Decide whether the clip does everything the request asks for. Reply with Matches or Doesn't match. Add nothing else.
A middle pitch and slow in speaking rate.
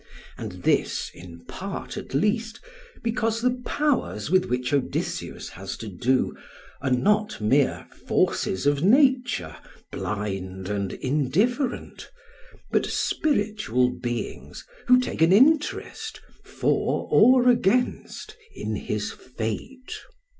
Matches